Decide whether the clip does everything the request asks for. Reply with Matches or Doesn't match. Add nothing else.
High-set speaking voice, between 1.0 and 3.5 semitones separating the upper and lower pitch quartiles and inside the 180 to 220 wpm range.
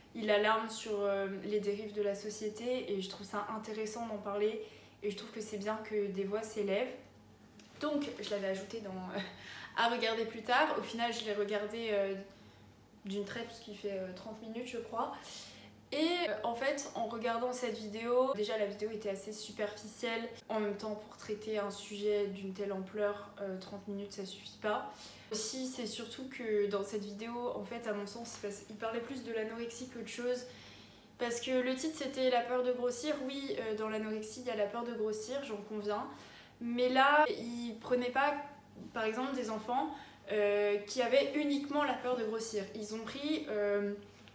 Matches